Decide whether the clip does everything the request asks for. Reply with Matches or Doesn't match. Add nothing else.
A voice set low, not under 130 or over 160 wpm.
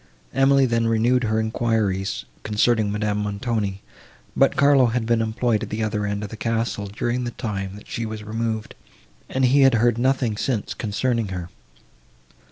Doesn't match